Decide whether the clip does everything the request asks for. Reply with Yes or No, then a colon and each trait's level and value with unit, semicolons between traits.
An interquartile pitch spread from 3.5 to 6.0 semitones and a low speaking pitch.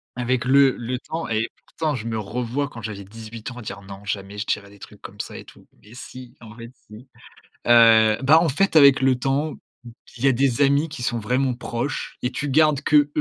Yes: average, 3.8 semitones; low, 125 Hz